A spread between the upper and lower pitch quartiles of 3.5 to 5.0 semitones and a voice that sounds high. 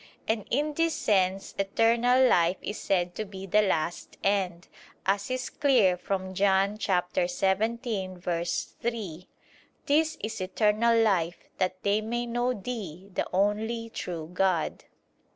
Yes: average, 4.0 semitones; high, 200 Hz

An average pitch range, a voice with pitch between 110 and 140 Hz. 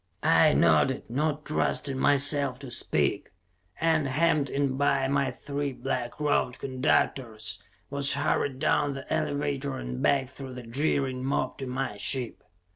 No: narrow, 1.8 semitones; low, 135 Hz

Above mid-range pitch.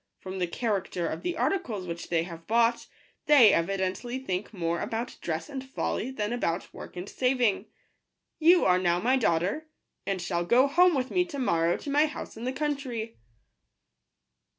Yes: high, 225 Hz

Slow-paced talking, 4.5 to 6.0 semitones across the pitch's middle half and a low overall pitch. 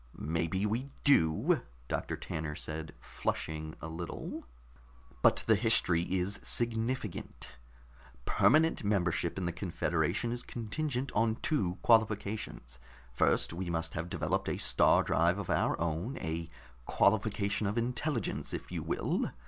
Yes: slow, 130 wpm; wide, 5.6 semitones; very low, 95 Hz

